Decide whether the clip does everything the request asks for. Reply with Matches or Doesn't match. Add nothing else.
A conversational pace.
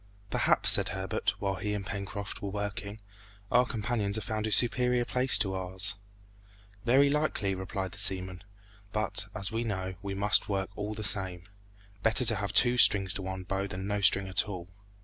Matches